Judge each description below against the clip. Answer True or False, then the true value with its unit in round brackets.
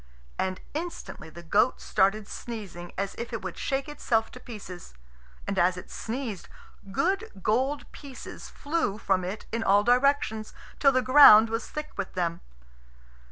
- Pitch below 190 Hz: False (220 Hz)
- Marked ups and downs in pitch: True (5.8 semitones)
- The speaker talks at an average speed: True (155 wpm)